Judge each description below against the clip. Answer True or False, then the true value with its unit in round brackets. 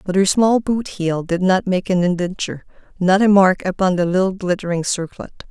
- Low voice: False (185 Hz)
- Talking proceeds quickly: False (195 wpm)